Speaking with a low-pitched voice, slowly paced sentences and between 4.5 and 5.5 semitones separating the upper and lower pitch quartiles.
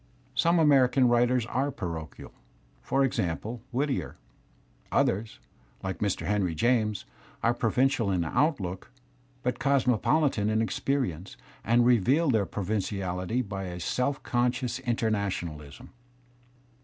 Yes: low, 115 Hz; slow, 105 wpm; average, 5.0 semitones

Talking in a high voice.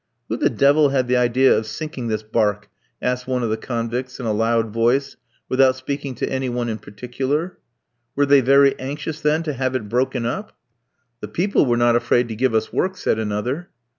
No: low, 125 Hz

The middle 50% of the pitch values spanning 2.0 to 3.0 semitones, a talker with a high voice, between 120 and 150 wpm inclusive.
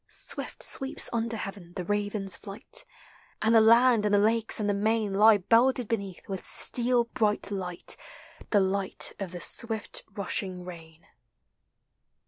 Yes: average, 2.7 semitones; high, 205 Hz; average, 145 wpm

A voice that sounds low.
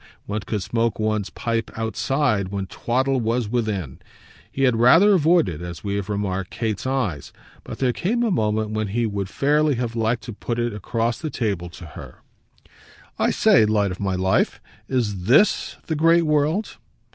Yes: low, 115 Hz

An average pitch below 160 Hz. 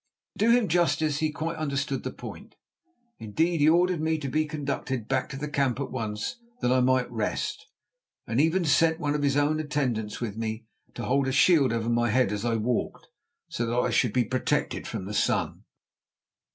Yes: low, 135 Hz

